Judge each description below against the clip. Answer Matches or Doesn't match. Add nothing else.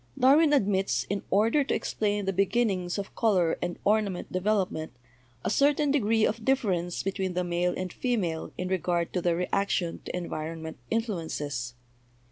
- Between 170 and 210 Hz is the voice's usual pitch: Matches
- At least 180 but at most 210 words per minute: Doesn't match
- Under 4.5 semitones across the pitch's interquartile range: Matches